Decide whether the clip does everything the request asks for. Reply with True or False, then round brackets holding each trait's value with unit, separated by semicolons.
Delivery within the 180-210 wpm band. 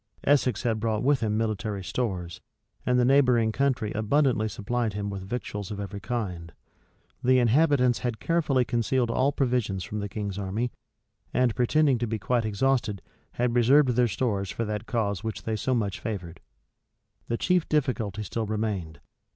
False (165 wpm)